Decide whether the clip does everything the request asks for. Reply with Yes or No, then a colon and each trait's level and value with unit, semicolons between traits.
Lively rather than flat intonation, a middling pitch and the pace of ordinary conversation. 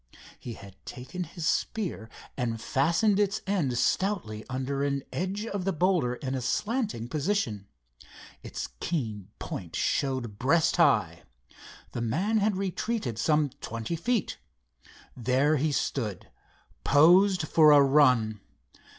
No: wide, 7.5 semitones; medium, 145 Hz; slow, 125 wpm